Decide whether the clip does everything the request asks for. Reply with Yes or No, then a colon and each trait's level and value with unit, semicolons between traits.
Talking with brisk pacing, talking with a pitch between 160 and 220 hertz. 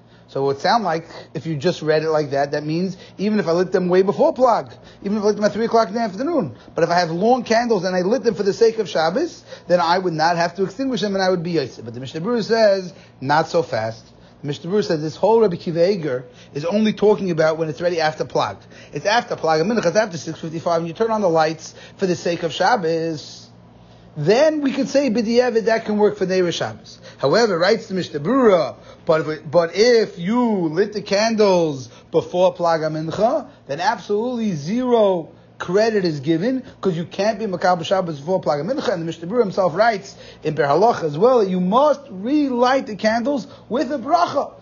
Yes: fast, 220 wpm; medium, 185 Hz